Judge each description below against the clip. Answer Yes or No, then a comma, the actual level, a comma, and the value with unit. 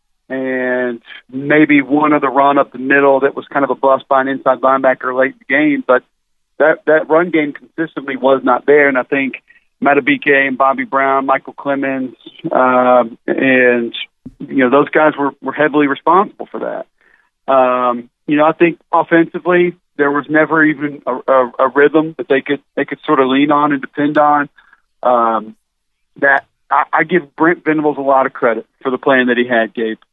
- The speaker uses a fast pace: No, average, 195 wpm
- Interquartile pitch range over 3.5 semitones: No, narrow, 2.6 semitones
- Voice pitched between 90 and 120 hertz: No, medium, 140 Hz